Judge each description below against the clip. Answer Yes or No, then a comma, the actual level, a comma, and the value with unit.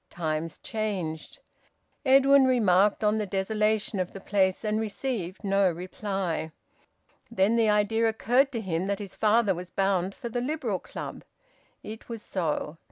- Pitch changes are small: No, average, 3.3 semitones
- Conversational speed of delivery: Yes, average, 150 wpm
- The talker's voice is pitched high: Yes, high, 205 Hz